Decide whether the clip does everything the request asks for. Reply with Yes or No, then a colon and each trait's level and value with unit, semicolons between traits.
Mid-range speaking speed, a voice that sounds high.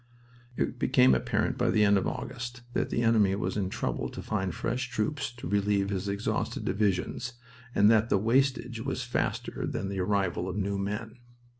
No: average, 180 wpm; low, 105 Hz